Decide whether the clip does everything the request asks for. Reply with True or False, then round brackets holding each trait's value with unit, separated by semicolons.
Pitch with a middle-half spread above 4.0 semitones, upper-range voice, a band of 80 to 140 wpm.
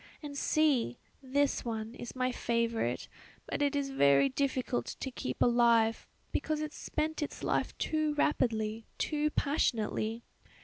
True (4.4 semitones; 255 Hz; 135 wpm)